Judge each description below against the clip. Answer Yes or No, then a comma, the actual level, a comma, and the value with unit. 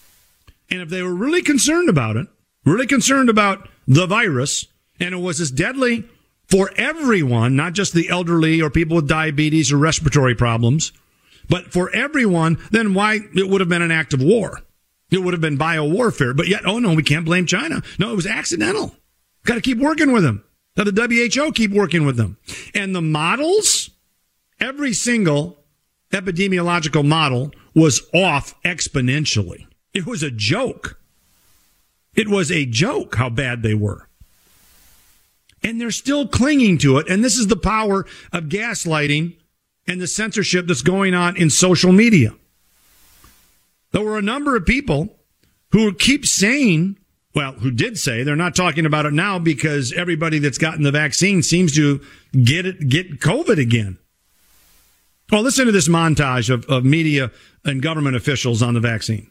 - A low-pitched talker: No, medium, 170 Hz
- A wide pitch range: Yes, wide, 6.0 semitones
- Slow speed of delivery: No, average, 165 wpm